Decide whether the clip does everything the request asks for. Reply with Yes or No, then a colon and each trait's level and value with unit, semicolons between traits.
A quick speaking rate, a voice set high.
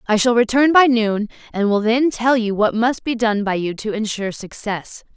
Yes: fast, 220 wpm; high, 225 Hz